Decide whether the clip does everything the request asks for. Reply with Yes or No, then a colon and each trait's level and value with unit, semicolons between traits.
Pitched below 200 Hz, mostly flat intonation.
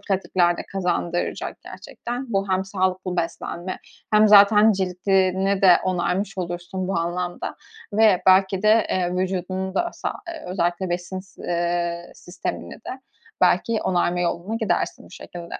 Yes: medium, 185 Hz; narrow, 1.9 semitones